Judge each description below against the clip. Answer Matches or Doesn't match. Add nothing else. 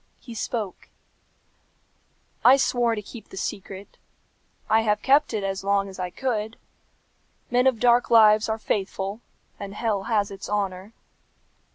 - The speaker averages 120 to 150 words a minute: Matches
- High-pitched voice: Matches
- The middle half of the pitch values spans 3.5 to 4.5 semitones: Doesn't match